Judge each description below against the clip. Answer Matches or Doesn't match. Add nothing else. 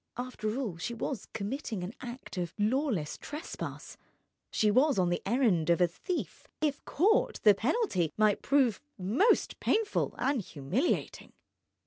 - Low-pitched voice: Doesn't match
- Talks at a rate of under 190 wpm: Matches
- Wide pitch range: Matches